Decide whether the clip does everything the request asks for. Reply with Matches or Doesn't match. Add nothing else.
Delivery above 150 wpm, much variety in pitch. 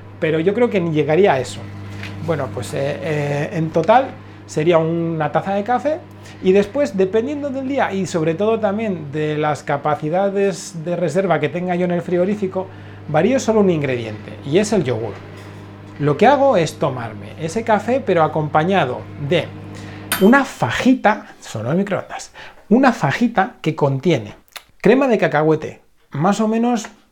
Matches